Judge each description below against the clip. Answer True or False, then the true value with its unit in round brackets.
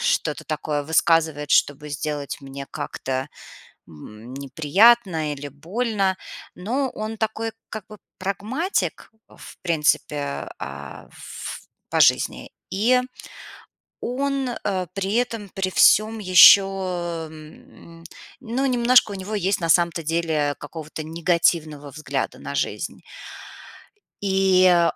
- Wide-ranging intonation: True (5.9 semitones)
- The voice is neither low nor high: True (180 Hz)